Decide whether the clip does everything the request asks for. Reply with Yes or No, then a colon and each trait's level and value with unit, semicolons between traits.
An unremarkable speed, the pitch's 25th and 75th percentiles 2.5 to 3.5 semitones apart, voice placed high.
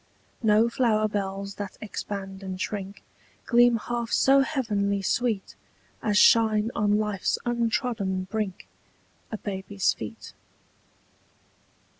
No: slow, 105 wpm; average, 2.8 semitones; high, 210 Hz